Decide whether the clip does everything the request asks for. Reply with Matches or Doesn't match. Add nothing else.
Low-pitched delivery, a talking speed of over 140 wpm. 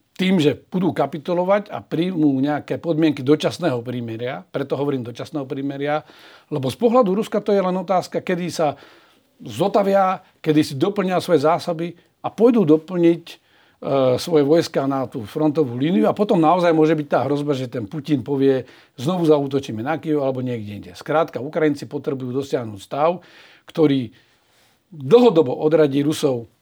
Doesn't match